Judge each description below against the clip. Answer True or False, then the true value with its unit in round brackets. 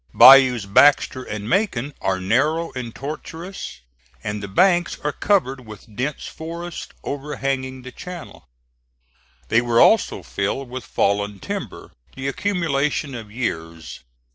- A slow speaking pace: True (125 wpm)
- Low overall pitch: True (130 Hz)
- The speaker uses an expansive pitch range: True (5.9 semitones)